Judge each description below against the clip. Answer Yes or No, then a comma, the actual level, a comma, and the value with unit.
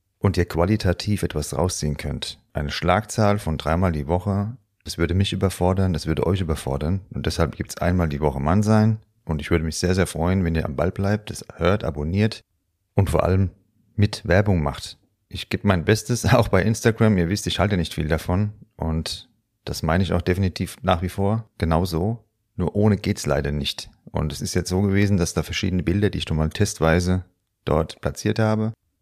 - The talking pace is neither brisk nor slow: No, fast, 200 wpm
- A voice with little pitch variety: No, average, 3.6 semitones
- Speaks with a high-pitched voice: No, very low, 95 Hz